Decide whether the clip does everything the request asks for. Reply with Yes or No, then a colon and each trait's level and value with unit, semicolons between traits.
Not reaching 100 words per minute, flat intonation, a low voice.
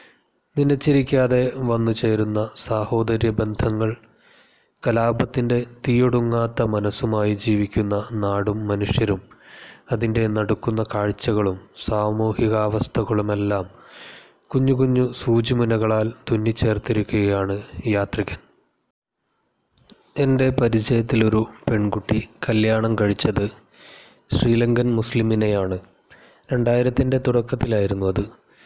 Yes: average, 65 wpm; narrow, 2.3 semitones; low, 110 Hz